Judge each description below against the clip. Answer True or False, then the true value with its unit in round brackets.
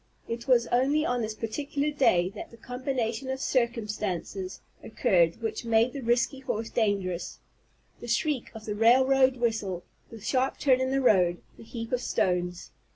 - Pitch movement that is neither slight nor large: True (3.7 semitones)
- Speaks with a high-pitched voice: True (235 Hz)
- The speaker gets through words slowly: False (160 wpm)